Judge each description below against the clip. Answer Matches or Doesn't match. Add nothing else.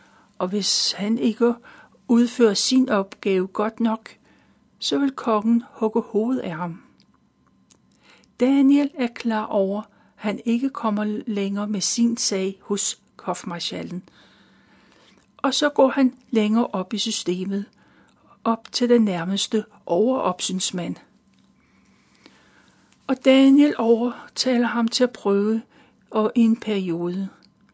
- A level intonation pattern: Doesn't match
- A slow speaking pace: Matches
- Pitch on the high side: Matches